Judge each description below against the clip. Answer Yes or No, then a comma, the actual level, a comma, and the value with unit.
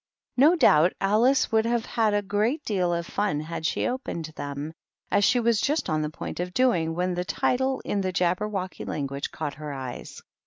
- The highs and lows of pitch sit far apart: Yes, wide, 6.2 semitones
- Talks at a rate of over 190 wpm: Yes, average, 200 wpm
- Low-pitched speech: No, medium, 185 Hz